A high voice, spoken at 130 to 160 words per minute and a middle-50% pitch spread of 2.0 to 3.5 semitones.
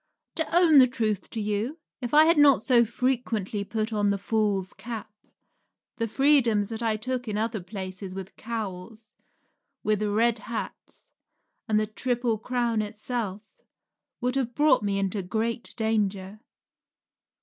Yes: high, 220 Hz; average, 140 wpm; average, 2.9 semitones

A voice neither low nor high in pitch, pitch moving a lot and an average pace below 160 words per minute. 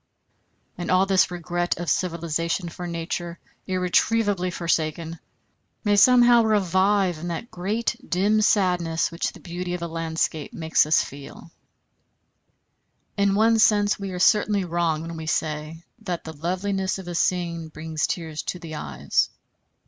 No: medium, 175 Hz; average, 3.0 semitones; average, 150 wpm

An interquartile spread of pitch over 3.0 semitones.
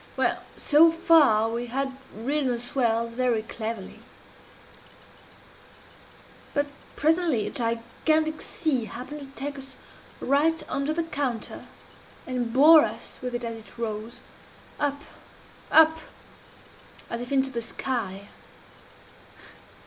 Yes: average, 4.3 semitones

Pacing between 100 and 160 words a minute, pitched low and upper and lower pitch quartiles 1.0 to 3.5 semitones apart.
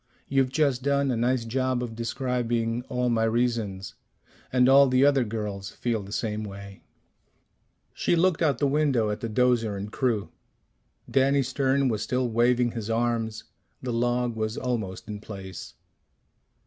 Yes: average, 155 wpm; low, 120 Hz; average, 2.8 semitones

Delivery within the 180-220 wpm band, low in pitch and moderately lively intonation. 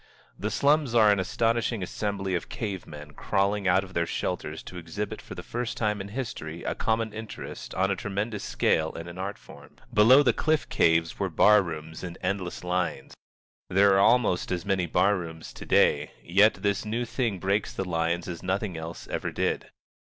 Yes: average, 190 wpm; very low, 95 Hz; average, 3.5 semitones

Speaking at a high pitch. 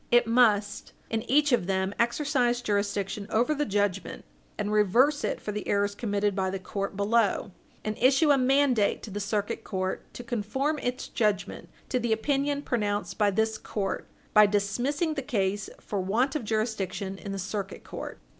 Yes: high, 215 Hz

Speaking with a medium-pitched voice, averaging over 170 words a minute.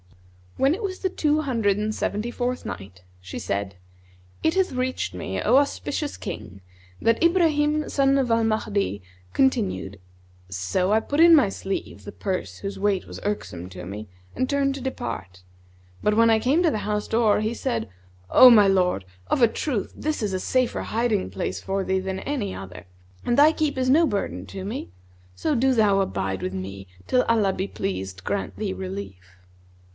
No: high, 210 Hz; average, 185 wpm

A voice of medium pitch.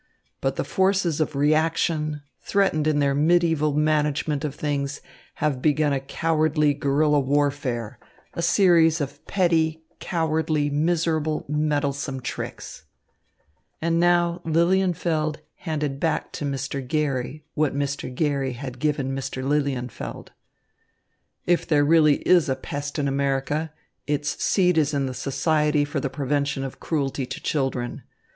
Yes: medium, 150 Hz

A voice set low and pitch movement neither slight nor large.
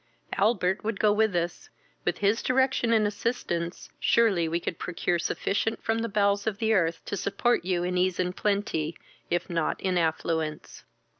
No: high, 195 Hz; average, 4.1 semitones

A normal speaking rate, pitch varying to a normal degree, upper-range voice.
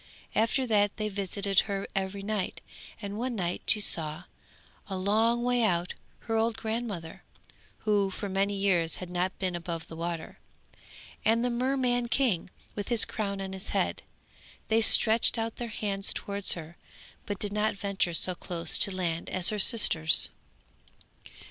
Yes: average, 160 wpm; average, 3.5 semitones; high, 200 Hz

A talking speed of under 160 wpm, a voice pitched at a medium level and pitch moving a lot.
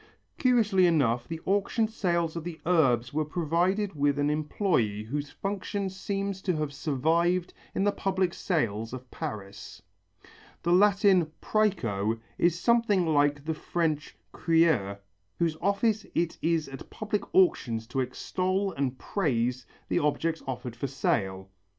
Yes: average, 140 wpm; medium, 165 Hz; wide, 6.2 semitones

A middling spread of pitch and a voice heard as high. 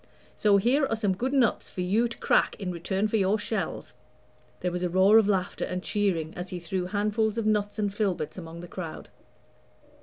Yes: average, 3.0 semitones; high, 200 Hz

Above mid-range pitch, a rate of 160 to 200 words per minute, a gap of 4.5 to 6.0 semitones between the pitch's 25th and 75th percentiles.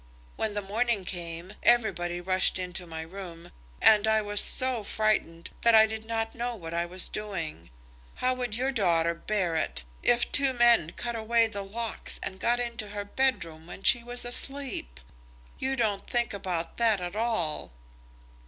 Yes: high, 210 Hz; average, 170 wpm; average, 5.1 semitones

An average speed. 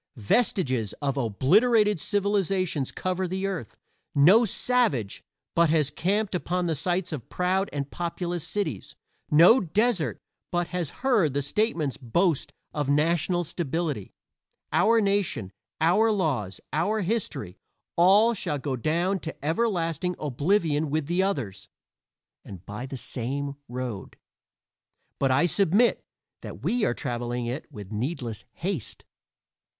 No: slow, 125 wpm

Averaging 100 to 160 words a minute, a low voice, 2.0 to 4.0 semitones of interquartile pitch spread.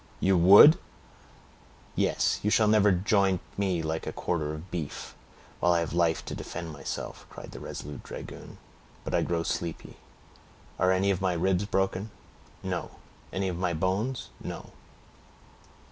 Yes: average, 150 wpm; very low, 90 Hz; narrow, 2.6 semitones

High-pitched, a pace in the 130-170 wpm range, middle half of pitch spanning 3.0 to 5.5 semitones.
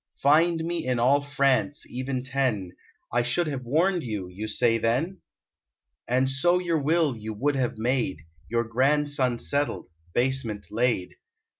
No: low, 130 Hz; average, 145 wpm; average, 3.8 semitones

